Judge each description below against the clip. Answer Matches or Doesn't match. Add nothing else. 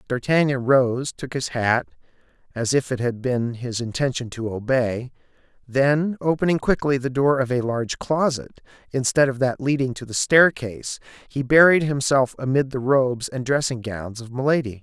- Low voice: Matches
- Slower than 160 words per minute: Doesn't match